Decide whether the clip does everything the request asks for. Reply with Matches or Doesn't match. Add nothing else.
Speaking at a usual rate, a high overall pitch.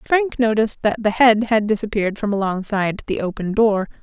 Matches